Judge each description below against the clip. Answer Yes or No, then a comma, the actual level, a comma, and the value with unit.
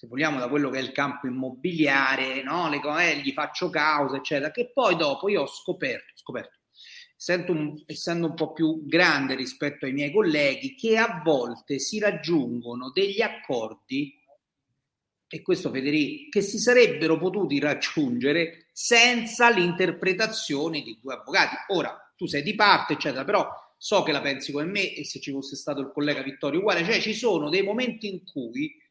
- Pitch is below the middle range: No, medium, 160 Hz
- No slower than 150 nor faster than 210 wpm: Yes, fast, 170 wpm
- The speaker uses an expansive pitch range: Yes, wide, 7.3 semitones